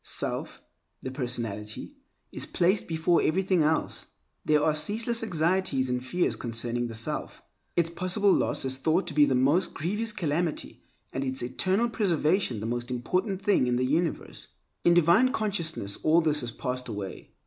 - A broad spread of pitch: Yes, wide, 6.5 semitones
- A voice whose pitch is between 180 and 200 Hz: No, medium, 155 Hz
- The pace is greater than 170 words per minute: No, average, 160 wpm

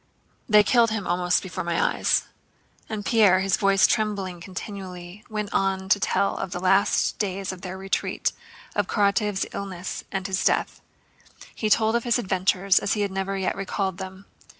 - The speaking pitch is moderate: No, high, 195 Hz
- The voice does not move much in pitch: Yes, narrow, 1.7 semitones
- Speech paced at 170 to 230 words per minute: Yes, average, 175 wpm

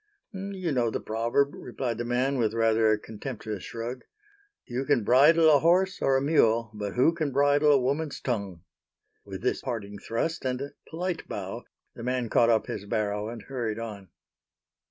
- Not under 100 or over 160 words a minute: No, average, 175 wpm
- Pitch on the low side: Yes, low, 125 Hz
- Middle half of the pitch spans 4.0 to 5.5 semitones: Yes, average, 4.4 semitones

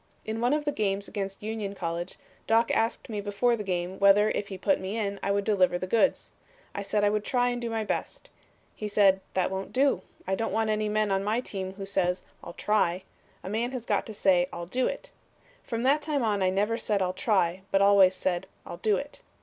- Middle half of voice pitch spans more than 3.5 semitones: No, average, 2.9 semitones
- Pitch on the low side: No, high, 205 Hz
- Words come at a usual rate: No, fast, 230 wpm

